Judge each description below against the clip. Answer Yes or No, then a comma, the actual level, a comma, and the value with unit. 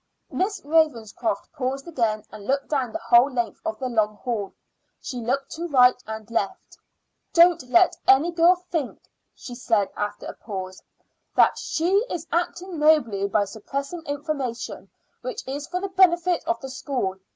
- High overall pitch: Yes, very high, 275 Hz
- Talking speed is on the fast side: No, average, 160 wpm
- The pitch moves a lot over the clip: Yes, wide, 6.7 semitones